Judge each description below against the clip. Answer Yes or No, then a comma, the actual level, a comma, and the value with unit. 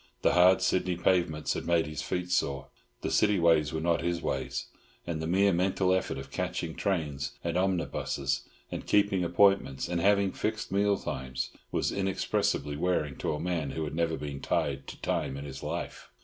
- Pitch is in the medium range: No, very low, 85 Hz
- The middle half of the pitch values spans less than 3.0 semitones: No, average, 4.0 semitones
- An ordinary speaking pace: Yes, average, 185 wpm